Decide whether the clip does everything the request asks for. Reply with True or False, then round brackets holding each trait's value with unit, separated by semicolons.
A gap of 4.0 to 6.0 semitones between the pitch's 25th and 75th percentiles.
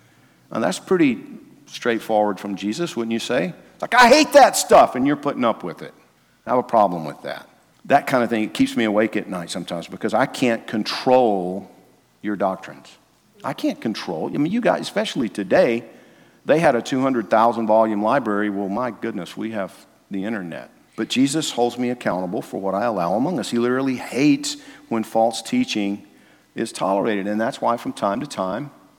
True (5.0 semitones)